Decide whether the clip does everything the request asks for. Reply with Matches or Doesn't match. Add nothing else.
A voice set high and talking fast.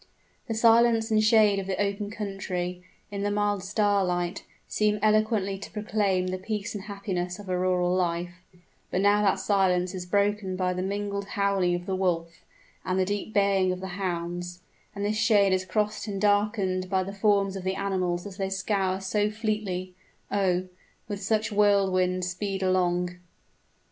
Doesn't match